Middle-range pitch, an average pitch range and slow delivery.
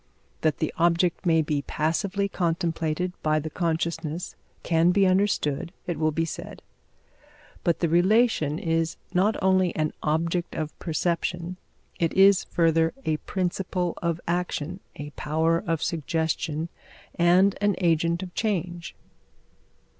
No: medium, 170 Hz; narrow, 2.1 semitones; slow, 130 wpm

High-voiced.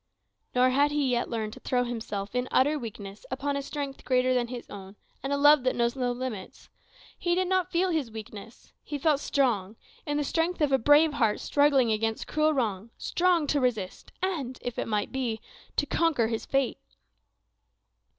Yes: very high, 255 Hz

